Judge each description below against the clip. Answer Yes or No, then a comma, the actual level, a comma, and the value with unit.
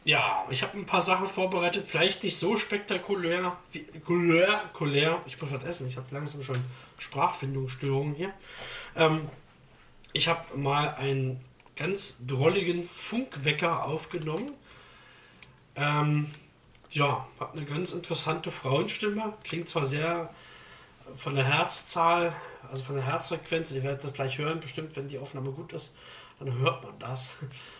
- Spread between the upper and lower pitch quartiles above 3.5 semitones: Yes, average, 4.2 semitones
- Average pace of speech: Yes, average, 140 wpm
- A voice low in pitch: No, medium, 155 Hz